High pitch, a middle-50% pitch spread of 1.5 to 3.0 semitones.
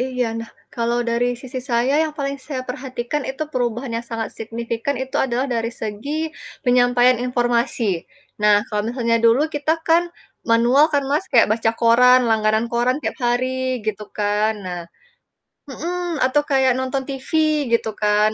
Yes: high, 245 Hz; average, 2.7 semitones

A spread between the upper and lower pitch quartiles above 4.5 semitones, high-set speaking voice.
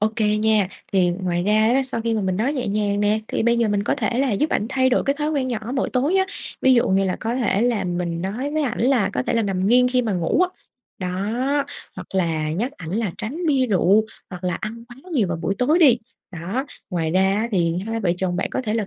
Yes: average, 5.1 semitones; high, 215 Hz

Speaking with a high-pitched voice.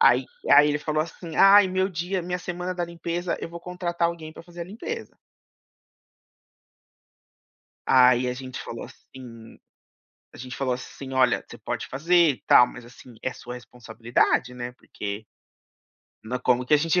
No: medium, 150 Hz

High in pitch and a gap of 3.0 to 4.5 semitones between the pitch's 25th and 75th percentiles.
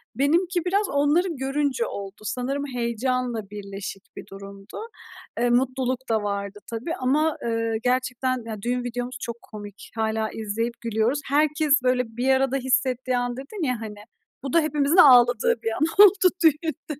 Yes: very high, 250 Hz; average, 3.9 semitones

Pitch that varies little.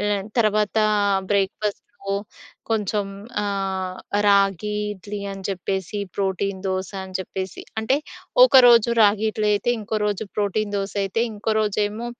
Yes: narrow, 1.6 semitones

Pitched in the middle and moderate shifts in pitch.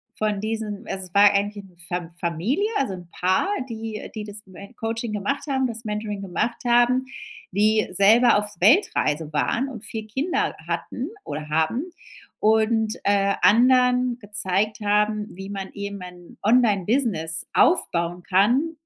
No: high, 210 Hz; average, 3.5 semitones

